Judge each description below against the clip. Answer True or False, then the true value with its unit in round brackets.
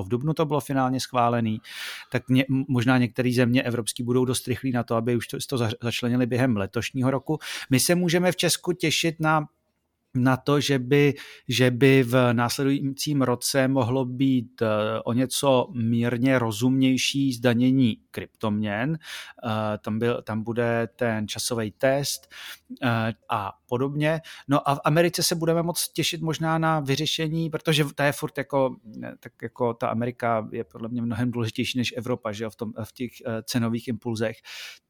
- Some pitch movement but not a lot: True (3.0 semitones)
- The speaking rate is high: False (160 wpm)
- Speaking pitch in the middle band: False (125 Hz)